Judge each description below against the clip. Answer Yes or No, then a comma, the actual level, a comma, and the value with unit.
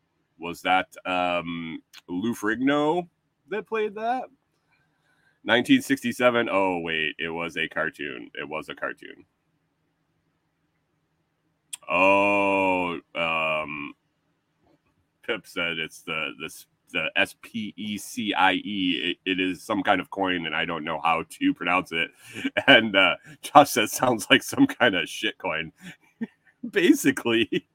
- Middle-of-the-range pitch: No, low, 120 Hz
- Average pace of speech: No, slow, 125 wpm